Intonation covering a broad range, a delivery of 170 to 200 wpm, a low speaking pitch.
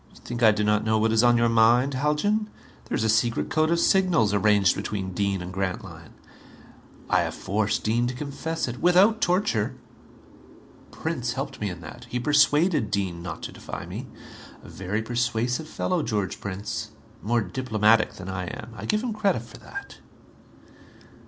Yes: wide, 6.0 semitones; average, 175 wpm; low, 115 Hz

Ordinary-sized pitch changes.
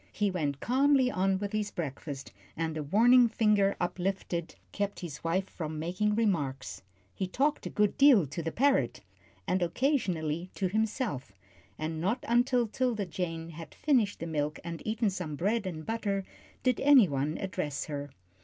No: wide, 5.8 semitones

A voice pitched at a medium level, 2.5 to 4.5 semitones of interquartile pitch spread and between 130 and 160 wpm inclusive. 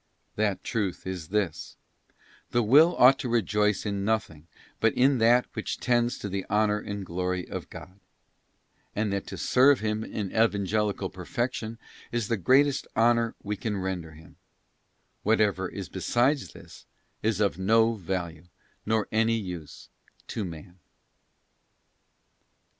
No: low, 105 Hz; average, 3.4 semitones; average, 140 wpm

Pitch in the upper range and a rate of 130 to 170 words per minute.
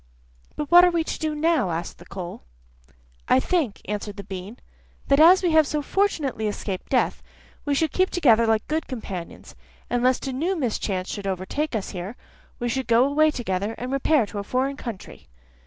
No: very high, 255 Hz; average, 190 wpm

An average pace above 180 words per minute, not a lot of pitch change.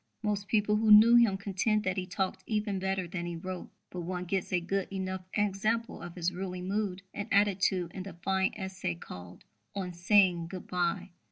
Yes: average, 190 wpm; narrow, 2.2 semitones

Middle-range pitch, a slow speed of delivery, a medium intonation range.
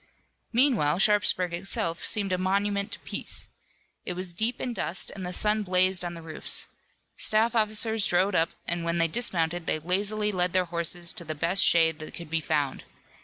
No: medium, 180 Hz; average, 185 wpm; average, 3.7 semitones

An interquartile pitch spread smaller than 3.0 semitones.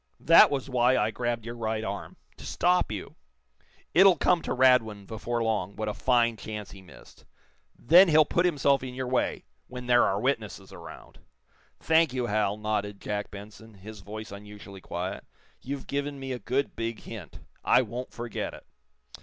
No: average, 3.8 semitones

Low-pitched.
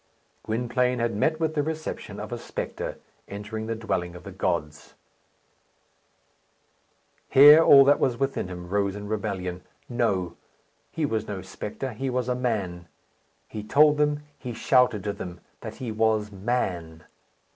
Yes: low, 110 Hz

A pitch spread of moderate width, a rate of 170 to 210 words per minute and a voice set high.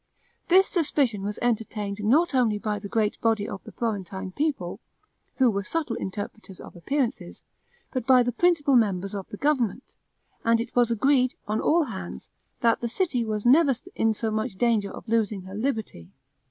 Yes: average, 4.0 semitones; average, 175 wpm; high, 225 Hz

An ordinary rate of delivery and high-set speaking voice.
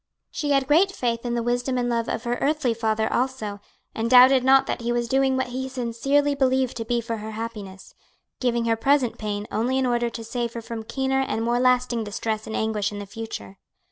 No: fast, 220 wpm; high, 240 Hz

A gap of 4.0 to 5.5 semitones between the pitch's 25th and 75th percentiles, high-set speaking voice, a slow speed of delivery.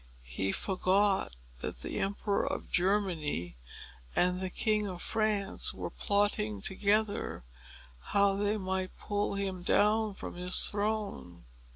No: narrow, 2.4 semitones; high, 195 Hz; slow, 125 wpm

